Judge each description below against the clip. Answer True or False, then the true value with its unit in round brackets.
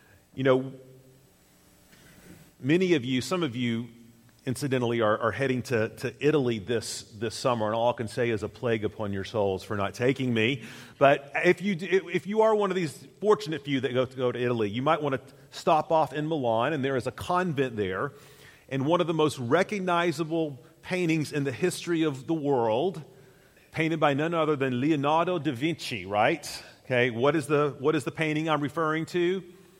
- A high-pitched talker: False (140 Hz)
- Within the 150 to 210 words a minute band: True (195 wpm)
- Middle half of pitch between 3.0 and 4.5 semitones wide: False (5.0 semitones)